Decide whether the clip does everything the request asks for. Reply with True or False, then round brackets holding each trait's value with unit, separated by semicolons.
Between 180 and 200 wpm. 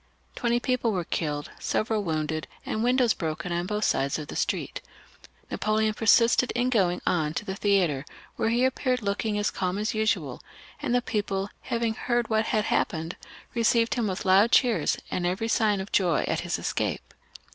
True (185 wpm)